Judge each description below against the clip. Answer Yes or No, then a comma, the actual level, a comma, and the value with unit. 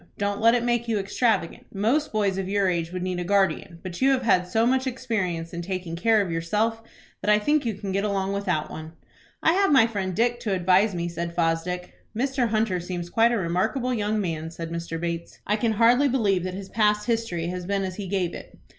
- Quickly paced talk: Yes, fast, 225 wpm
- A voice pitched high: Yes, high, 200 Hz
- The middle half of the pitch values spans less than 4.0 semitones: No, average, 4.3 semitones